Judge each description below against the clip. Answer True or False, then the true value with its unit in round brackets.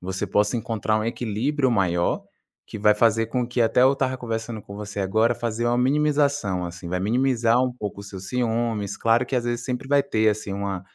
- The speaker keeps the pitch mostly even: False (3.4 semitones)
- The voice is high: False (115 Hz)